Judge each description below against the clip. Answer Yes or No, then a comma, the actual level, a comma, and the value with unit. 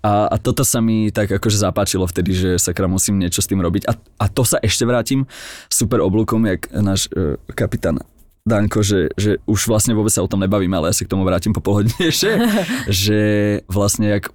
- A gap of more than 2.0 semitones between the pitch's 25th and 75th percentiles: Yes, narrow, 2.4 semitones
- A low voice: Yes, low, 105 Hz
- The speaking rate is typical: No, fast, 200 wpm